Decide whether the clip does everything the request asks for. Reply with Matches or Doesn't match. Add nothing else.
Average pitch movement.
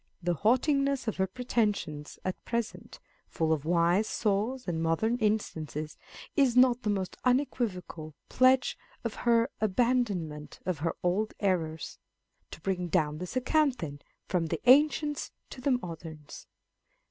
Doesn't match